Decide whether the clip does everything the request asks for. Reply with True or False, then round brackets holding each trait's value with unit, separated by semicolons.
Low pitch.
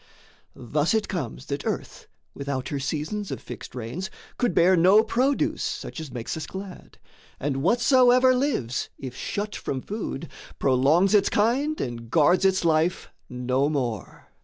False (165 Hz)